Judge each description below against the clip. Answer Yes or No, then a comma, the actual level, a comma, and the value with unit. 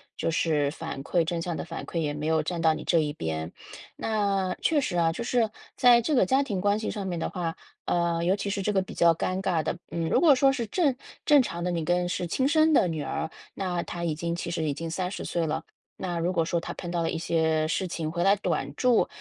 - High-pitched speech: No, medium, 175 Hz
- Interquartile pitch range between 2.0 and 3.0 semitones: No, average, 3.7 semitones